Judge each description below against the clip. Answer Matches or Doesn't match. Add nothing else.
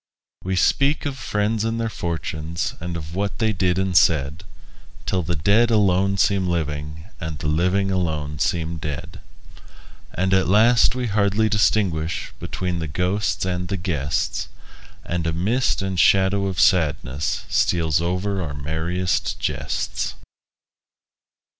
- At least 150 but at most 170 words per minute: Doesn't match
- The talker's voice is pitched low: Matches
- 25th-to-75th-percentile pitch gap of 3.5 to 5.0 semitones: Matches